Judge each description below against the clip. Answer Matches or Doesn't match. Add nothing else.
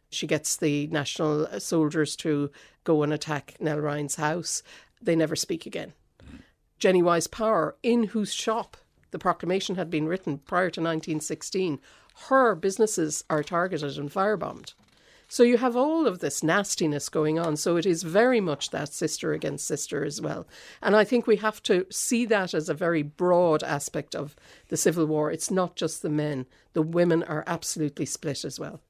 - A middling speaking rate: Matches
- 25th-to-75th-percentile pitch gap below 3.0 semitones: Doesn't match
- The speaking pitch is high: Doesn't match